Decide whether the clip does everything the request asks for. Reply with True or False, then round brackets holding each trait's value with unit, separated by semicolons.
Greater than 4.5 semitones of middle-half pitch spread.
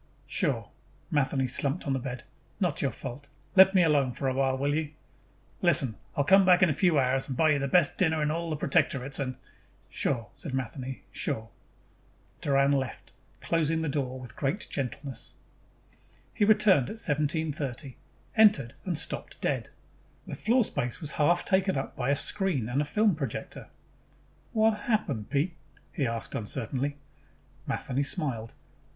False (4.2 semitones)